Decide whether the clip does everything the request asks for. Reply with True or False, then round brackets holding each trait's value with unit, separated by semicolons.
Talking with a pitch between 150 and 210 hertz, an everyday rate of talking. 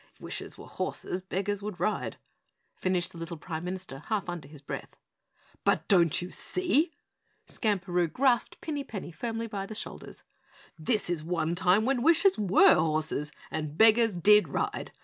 True (190 Hz; 160 wpm)